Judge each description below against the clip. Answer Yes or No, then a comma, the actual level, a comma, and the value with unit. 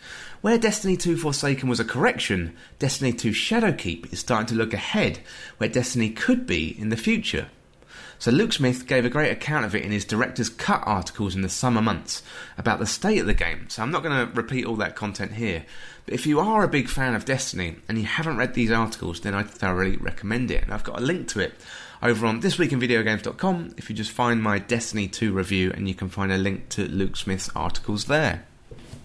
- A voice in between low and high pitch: No, low, 115 Hz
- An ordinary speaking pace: No, fast, 215 wpm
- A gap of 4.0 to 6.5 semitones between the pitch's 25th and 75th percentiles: Yes, average, 4.4 semitones